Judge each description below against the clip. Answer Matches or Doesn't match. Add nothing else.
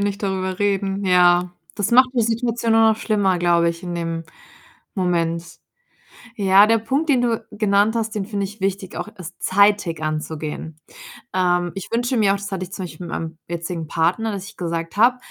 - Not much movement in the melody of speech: Doesn't match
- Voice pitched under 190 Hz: Doesn't match